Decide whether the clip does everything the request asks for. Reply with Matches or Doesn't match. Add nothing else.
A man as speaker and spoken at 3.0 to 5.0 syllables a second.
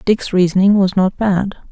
Doesn't match